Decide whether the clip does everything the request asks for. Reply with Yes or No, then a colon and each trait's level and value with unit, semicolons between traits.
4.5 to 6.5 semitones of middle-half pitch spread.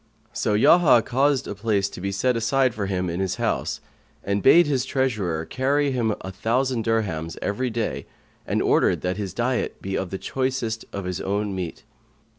Yes: average, 5.1 semitones